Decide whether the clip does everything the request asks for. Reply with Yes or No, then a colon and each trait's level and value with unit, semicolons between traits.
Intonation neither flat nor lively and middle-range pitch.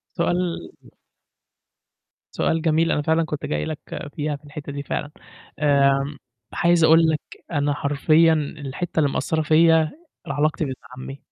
No: narrow, 2.1 semitones; medium, 150 Hz